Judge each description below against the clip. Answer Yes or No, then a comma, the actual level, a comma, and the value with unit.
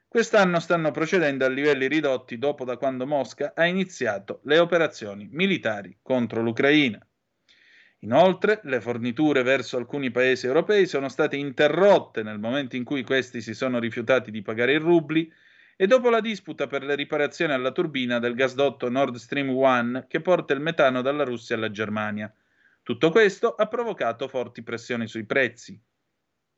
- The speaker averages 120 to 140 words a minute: No, average, 155 wpm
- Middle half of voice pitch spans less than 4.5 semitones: No, average, 5.0 semitones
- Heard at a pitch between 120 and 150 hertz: Yes, low, 135 Hz